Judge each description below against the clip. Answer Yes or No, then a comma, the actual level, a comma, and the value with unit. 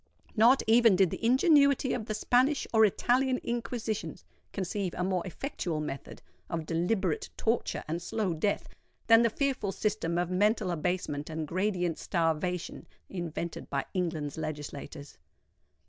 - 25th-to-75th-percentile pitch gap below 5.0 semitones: No, wide, 5.6 semitones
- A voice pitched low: No, high, 190 Hz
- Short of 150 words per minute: Yes, slow, 135 wpm